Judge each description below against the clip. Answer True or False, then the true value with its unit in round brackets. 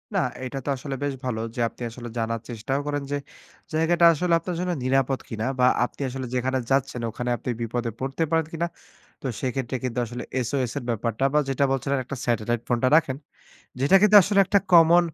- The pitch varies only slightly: False (3.7 semitones)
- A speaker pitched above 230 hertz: False (135 Hz)